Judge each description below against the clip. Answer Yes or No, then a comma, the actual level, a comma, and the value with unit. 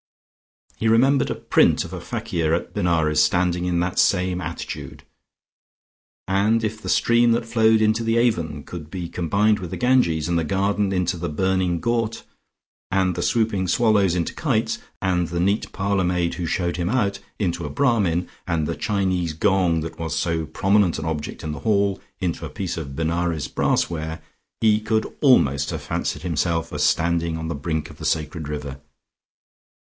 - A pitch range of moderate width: Yes, average, 4.0 semitones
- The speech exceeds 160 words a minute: Yes, average, 175 wpm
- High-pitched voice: No, very low, 90 Hz